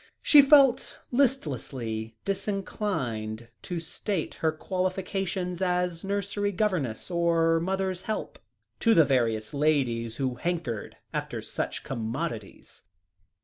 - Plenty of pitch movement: Yes, wide, 7.5 semitones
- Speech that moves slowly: Yes, slow, 105 wpm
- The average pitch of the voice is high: No, medium, 170 Hz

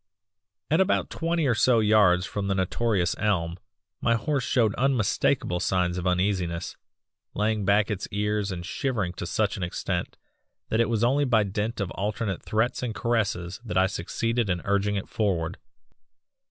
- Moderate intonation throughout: Yes, average, 3.8 semitones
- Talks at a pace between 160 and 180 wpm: Yes, average, 165 wpm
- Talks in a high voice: No, low, 105 Hz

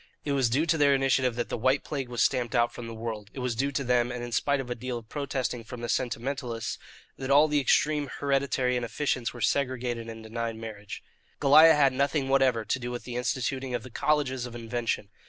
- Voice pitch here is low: Yes, low, 125 Hz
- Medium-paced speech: No, fast, 225 wpm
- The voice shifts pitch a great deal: No, average, 2.7 semitones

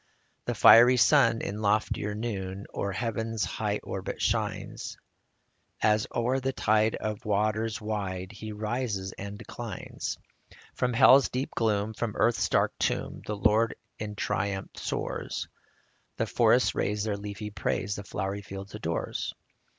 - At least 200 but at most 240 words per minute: No, average, 140 wpm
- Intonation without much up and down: Yes, narrow, 2.1 semitones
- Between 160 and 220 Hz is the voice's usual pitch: No, low, 105 Hz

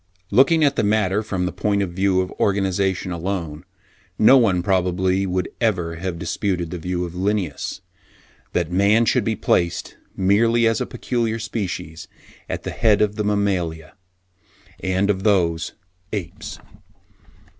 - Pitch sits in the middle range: No, very low, 95 Hz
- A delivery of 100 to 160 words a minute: Yes, average, 145 wpm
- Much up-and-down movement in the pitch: No, average, 2.9 semitones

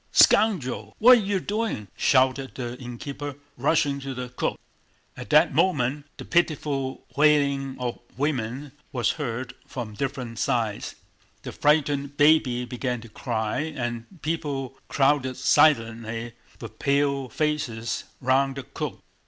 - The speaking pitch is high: No, low, 135 Hz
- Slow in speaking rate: Yes, slow, 130 wpm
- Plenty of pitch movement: No, average, 3.3 semitones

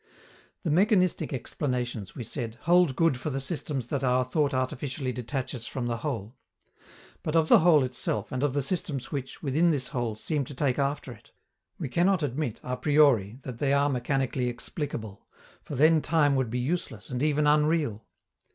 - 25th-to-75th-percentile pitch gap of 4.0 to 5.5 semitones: No, average, 3.4 semitones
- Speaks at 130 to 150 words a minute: No, average, 180 wpm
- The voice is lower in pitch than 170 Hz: Yes, low, 135 Hz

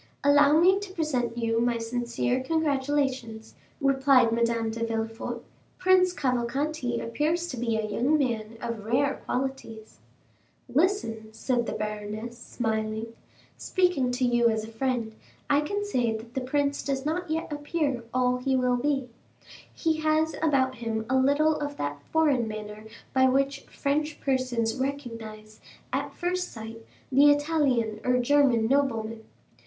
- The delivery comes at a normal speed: Yes, average, 145 wpm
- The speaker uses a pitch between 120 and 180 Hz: No, very high, 255 Hz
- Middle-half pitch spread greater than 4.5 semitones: No, average, 4.2 semitones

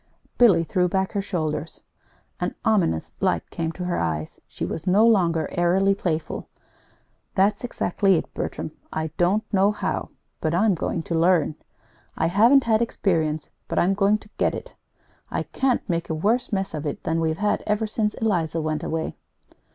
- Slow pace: No, average, 175 wpm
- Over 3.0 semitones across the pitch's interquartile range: Yes, average, 4.3 semitones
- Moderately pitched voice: Yes, medium, 180 Hz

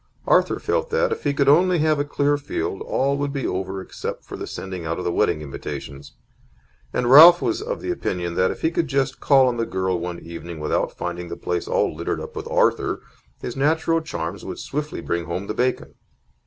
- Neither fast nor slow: No, fast, 210 wpm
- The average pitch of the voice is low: Yes, low, 130 Hz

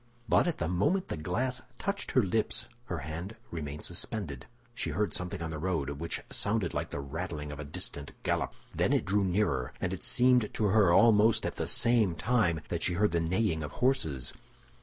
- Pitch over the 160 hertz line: No, very low, 90 Hz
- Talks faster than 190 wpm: Yes, average, 200 wpm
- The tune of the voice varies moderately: No, wide, 5.7 semitones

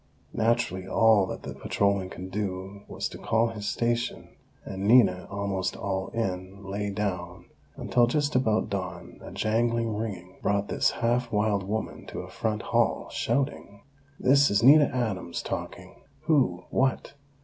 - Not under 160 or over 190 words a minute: No, average, 150 wpm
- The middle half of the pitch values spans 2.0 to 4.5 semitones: Yes, average, 3.5 semitones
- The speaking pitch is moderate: No, low, 105 Hz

